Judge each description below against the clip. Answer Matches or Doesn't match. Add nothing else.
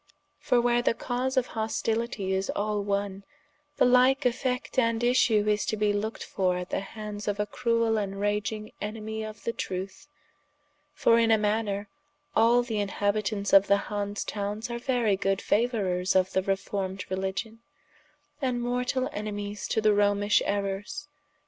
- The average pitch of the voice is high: Matches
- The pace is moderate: Matches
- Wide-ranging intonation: Doesn't match